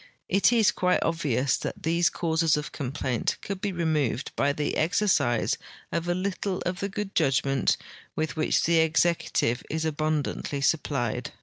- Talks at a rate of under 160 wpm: Yes, average, 150 wpm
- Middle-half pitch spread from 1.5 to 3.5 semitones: No, average, 4.0 semitones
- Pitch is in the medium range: Yes, medium, 160 Hz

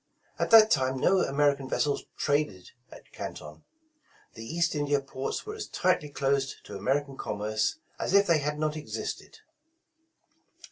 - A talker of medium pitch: Yes, medium, 145 Hz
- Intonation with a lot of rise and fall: No, average, 3.7 semitones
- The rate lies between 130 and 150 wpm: Yes, average, 145 wpm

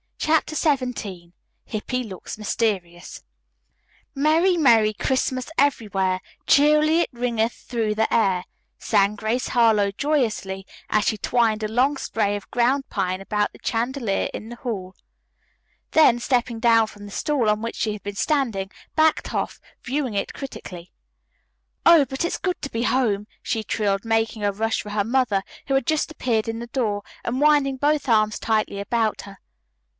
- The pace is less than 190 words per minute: Yes, average, 160 wpm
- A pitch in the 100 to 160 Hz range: No, high, 225 Hz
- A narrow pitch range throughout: No, average, 4.4 semitones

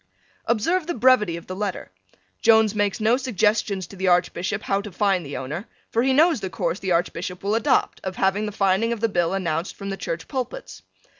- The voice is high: Yes, high, 200 Hz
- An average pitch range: Yes, average, 3.6 semitones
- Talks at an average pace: No, fast, 210 wpm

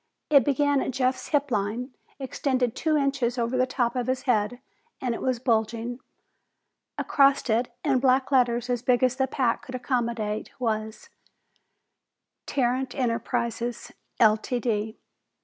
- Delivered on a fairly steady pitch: Yes, narrow, 2.0 semitones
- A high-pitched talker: Yes, high, 245 Hz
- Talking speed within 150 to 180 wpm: No, slow, 135 wpm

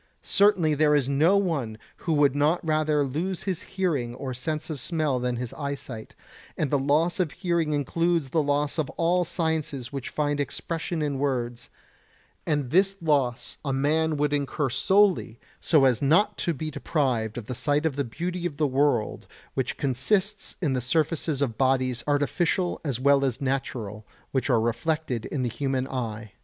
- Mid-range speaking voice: Yes, medium, 145 Hz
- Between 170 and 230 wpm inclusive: Yes, average, 175 wpm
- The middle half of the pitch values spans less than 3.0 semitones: No, average, 3.7 semitones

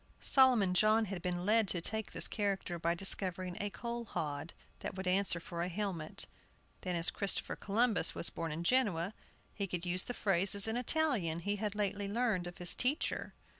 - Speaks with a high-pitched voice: Yes, high, 195 Hz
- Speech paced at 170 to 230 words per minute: Yes, average, 185 wpm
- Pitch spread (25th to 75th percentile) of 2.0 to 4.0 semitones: Yes, average, 3.6 semitones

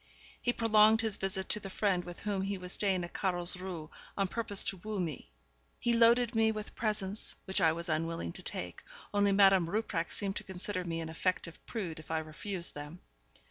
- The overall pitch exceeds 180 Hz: Yes, high, 190 Hz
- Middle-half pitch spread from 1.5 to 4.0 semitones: Yes, average, 3.6 semitones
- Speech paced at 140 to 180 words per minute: No, average, 195 wpm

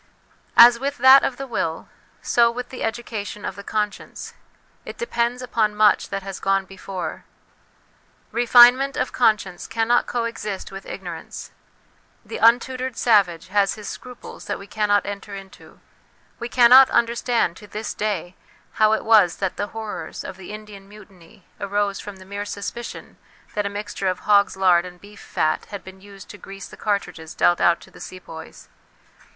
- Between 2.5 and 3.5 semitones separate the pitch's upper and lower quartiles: Yes, average, 3.2 semitones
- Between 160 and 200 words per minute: Yes, average, 170 wpm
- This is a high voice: Yes, high, 205 Hz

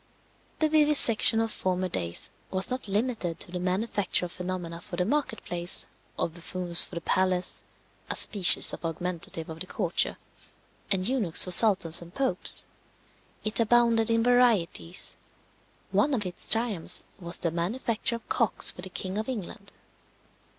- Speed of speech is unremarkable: Yes, average, 155 wpm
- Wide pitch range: No, average, 4.6 semitones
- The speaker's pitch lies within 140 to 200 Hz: Yes, high, 190 Hz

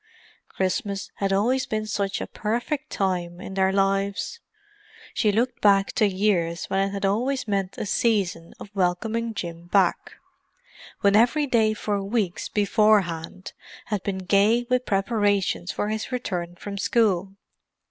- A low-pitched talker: No, high, 200 Hz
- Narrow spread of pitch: Yes, narrow, 2.3 semitones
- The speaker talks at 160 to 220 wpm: No, average, 145 wpm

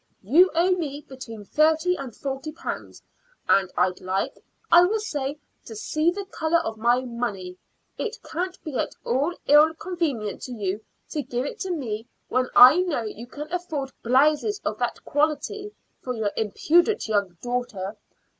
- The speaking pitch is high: Yes, very high, 275 Hz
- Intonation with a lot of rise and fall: Yes, wide, 6.9 semitones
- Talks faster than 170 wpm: No, average, 155 wpm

